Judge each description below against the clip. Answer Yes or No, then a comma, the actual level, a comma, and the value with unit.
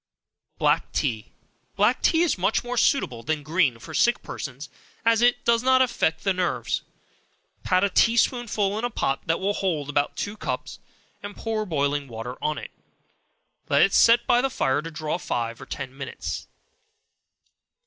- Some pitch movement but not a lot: No, wide, 8.4 semitones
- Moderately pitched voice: Yes, medium, 180 Hz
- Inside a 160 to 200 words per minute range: Yes, average, 170 wpm